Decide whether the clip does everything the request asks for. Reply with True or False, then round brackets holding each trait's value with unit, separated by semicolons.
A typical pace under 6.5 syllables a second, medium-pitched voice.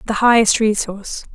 False (5.5 syllables/s; 215 Hz)